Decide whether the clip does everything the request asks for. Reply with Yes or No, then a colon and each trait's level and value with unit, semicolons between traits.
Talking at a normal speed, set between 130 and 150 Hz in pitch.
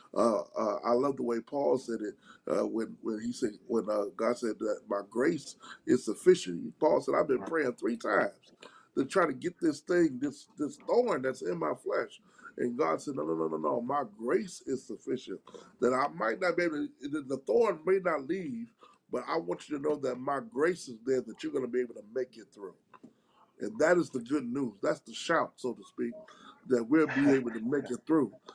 No: fast, 225 wpm; low, 135 Hz